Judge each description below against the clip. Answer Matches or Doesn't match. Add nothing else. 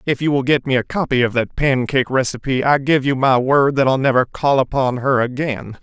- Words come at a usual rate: Doesn't match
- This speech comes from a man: Matches